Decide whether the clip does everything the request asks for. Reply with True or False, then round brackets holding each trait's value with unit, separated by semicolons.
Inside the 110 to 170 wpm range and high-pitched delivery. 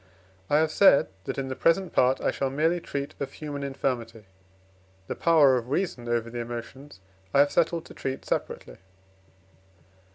False (165 wpm; 140 Hz)